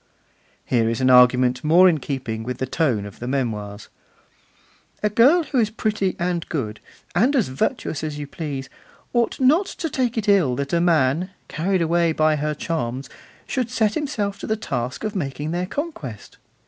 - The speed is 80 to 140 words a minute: No, average, 180 wpm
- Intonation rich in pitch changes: Yes, wide, 8.3 semitones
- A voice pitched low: No, medium, 160 Hz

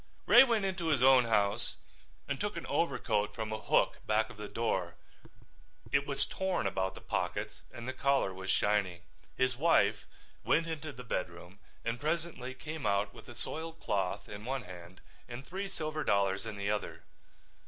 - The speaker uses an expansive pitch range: Yes, wide, 7.1 semitones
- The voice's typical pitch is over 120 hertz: No, low, 115 Hz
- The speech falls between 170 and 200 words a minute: Yes, average, 175 wpm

